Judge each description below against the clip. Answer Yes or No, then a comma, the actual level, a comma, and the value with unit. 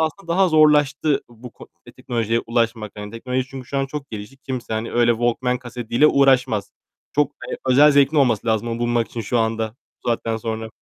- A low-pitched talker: Yes, low, 120 Hz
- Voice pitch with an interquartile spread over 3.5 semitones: No, average, 3.2 semitones